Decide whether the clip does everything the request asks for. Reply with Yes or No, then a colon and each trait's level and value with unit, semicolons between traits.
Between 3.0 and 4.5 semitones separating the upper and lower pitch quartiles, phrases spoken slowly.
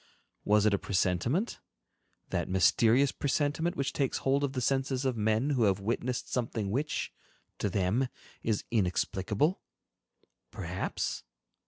No: average, 5.2 semitones; slow, 125 wpm